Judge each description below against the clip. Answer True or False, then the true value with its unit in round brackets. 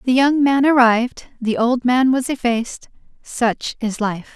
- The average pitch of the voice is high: True (245 Hz)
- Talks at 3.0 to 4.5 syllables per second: True (4.2 syllables/s)